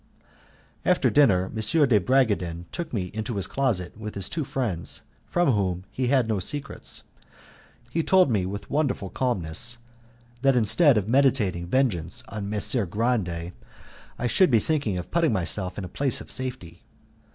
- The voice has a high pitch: No, low, 110 Hz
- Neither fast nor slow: Yes, average, 160 wpm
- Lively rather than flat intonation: Yes, wide, 6.3 semitones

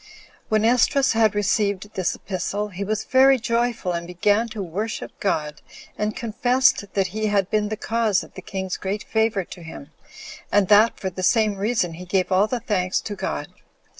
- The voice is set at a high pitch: Yes, high, 205 Hz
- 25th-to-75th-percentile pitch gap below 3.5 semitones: Yes, average, 2.8 semitones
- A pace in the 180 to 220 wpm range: Yes, average, 190 wpm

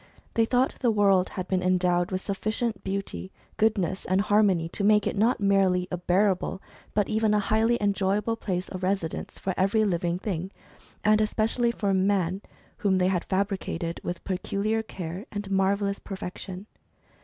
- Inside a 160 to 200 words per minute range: Yes, average, 170 wpm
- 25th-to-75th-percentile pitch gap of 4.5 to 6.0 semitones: No, narrow, 2.4 semitones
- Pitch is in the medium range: No, high, 195 Hz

